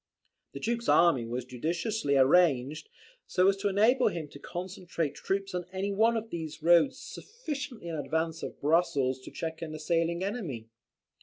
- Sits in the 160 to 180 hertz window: Yes, medium, 170 Hz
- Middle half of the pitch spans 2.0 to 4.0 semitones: No, average, 4.8 semitones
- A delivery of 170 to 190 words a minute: No, average, 160 wpm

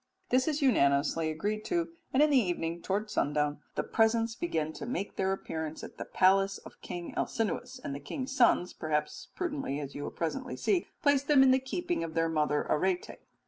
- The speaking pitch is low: No, high, 195 Hz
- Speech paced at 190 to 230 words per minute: Yes, average, 195 wpm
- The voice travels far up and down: Yes, wide, 8.7 semitones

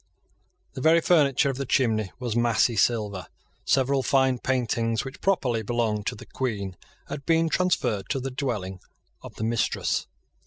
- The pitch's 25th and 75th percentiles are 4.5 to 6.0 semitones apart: No, average, 3.6 semitones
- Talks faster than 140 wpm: Yes, average, 155 wpm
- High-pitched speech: No, low, 125 Hz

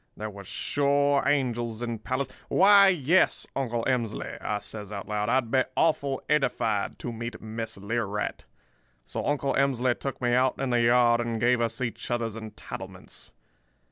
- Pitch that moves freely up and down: No, average, 3.2 semitones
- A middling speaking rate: Yes, average, 155 wpm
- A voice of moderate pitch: No, low, 120 Hz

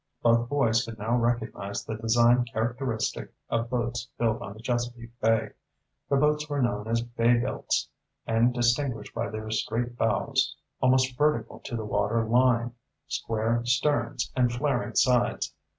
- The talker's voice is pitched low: Yes, low, 120 Hz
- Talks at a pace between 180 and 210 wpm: No, average, 150 wpm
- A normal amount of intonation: No, narrow, 1.6 semitones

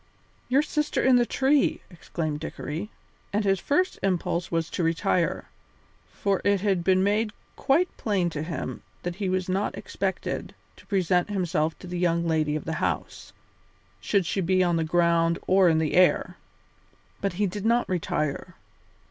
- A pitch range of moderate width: Yes, average, 3.4 semitones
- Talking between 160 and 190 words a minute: Yes, average, 165 wpm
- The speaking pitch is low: No, medium, 180 Hz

